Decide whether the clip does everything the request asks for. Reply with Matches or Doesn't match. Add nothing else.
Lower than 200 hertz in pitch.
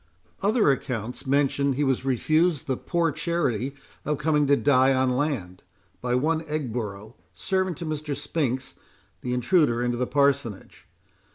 Matches